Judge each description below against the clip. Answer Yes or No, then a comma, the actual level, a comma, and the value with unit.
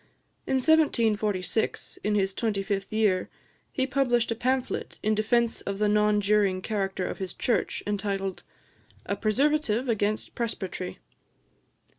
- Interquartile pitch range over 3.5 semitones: No, average, 3.1 semitones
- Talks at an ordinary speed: No, slow, 130 wpm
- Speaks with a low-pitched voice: No, high, 210 Hz